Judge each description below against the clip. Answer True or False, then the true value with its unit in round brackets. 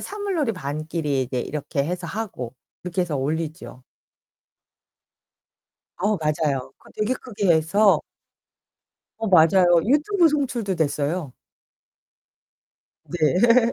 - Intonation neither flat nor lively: False (6.7 semitones)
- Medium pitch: True (175 Hz)